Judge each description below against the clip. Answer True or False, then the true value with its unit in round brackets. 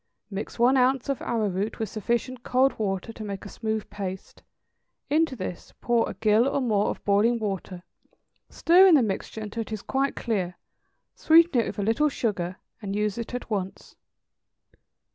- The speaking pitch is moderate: False (220 Hz)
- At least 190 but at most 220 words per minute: False (175 wpm)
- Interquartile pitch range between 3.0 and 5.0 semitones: True (4.0 semitones)